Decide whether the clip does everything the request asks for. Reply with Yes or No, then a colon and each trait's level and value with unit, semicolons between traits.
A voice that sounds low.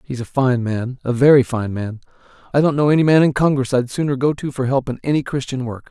Yes: low, 130 Hz